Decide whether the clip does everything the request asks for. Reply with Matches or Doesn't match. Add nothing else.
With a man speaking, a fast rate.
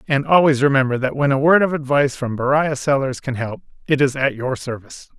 Matches